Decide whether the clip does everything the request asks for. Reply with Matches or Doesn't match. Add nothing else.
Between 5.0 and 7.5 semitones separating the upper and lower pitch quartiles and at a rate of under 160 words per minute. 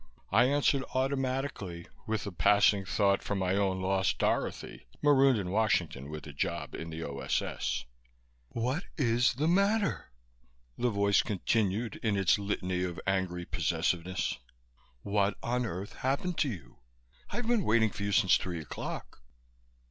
Matches